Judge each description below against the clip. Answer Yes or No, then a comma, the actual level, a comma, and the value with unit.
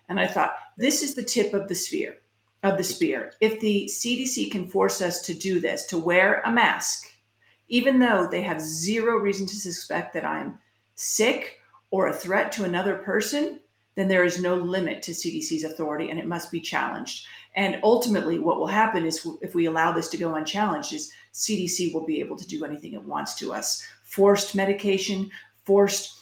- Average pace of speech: Yes, average, 190 wpm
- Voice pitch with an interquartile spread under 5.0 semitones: Yes, average, 3.8 semitones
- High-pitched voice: Yes, high, 195 Hz